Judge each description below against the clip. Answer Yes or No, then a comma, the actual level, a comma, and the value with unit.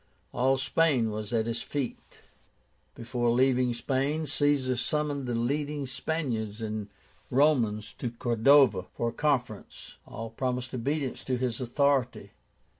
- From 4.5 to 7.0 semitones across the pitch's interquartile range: No, average, 3.3 semitones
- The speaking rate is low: Yes, slow, 125 wpm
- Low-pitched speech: Yes, low, 125 Hz